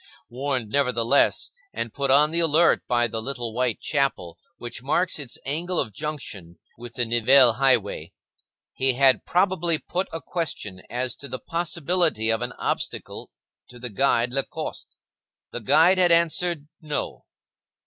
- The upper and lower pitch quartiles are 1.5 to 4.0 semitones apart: No, average, 5.0 semitones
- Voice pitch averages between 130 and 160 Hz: Yes, low, 135 Hz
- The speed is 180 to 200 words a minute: No, average, 150 wpm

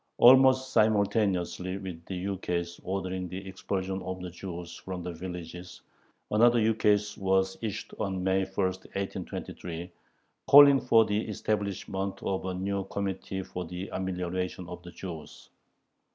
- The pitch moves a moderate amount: No, narrow, 2.0 semitones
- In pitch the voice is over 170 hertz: No, very low, 95 Hz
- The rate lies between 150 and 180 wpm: No, slow, 135 wpm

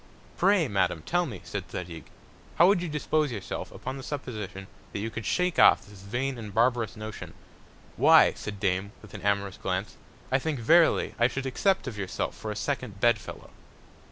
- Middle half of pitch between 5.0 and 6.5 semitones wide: Yes, wide, 5.6 semitones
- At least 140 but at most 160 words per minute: No, average, 190 wpm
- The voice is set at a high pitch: No, low, 110 Hz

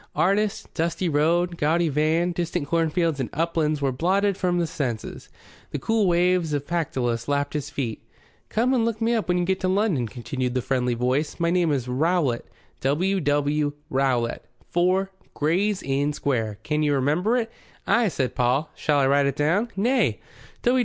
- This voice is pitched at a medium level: Yes, medium, 155 Hz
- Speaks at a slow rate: No, average, 175 wpm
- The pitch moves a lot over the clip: No, average, 4.7 semitones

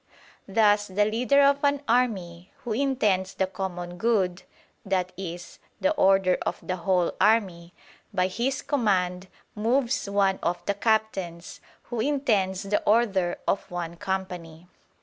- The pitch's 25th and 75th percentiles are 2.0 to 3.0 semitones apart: No, average, 3.9 semitones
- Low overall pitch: No, high, 195 Hz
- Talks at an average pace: No, slow, 130 wpm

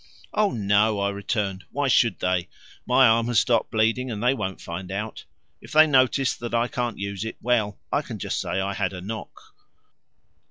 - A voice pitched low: Yes, low, 110 Hz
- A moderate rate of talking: Yes, average, 195 wpm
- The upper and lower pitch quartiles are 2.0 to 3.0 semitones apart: No, average, 3.6 semitones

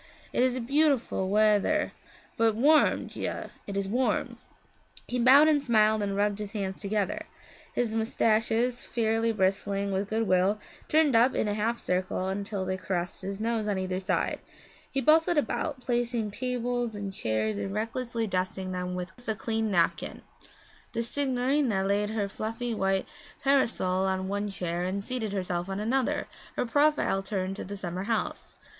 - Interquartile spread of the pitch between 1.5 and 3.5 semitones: No, average, 3.9 semitones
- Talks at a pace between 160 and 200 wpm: Yes, average, 165 wpm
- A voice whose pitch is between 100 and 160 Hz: No, high, 215 Hz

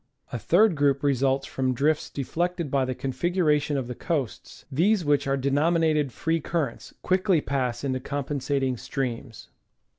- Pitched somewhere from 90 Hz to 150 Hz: Yes, medium, 140 Hz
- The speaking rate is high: No, average, 155 wpm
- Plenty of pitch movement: No, average, 3.6 semitones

